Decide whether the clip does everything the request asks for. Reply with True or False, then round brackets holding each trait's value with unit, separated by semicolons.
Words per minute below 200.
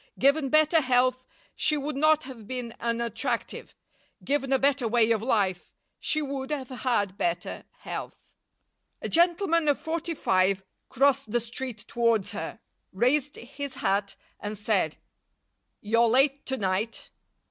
True (135 wpm)